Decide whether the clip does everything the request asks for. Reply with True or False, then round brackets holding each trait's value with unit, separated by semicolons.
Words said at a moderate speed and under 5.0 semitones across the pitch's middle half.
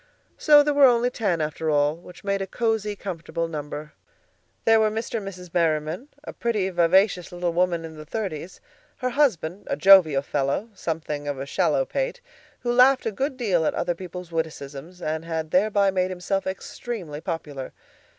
False (175 wpm; 5.4 semitones)